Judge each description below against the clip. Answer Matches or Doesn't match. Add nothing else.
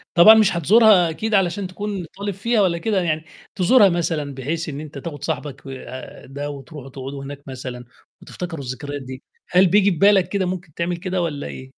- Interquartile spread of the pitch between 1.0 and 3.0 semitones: Doesn't match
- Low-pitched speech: Doesn't match